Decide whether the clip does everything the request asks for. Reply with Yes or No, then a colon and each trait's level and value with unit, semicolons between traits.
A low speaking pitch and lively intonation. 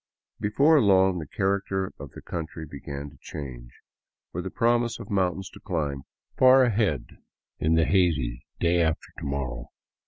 Yes: very low, 85 Hz; wide, 5.8 semitones